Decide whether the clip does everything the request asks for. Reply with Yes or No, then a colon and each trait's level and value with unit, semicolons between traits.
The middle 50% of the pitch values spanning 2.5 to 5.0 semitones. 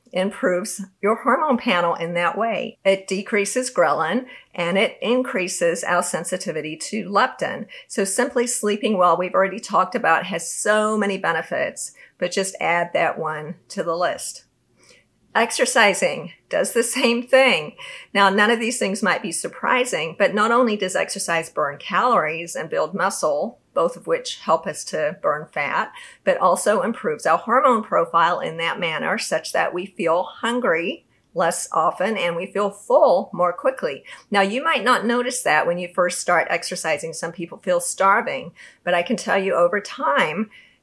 No: wide, 5.4 semitones